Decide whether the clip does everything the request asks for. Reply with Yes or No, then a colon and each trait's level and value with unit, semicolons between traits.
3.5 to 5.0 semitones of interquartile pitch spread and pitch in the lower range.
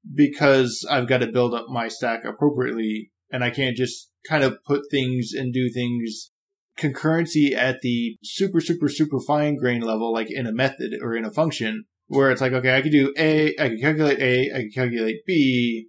Yes: average, 3.9 semitones; low, 130 Hz